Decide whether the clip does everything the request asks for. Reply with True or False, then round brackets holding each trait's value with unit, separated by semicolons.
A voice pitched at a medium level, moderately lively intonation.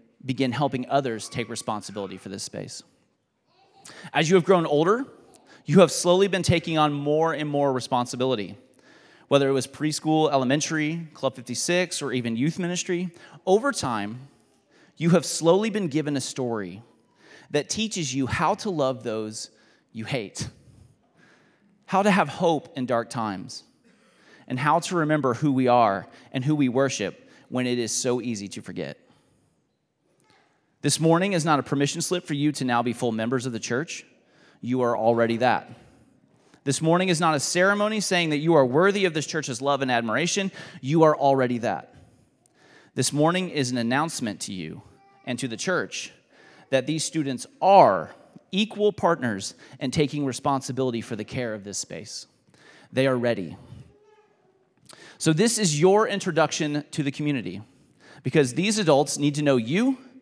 True (145 Hz; 5.0 semitones)